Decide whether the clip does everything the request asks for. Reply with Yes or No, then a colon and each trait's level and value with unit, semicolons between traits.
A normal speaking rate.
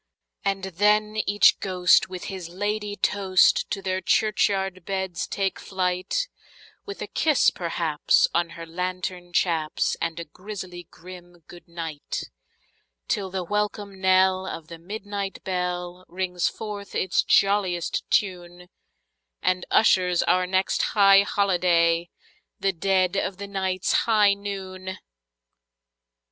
No: slow, 120 wpm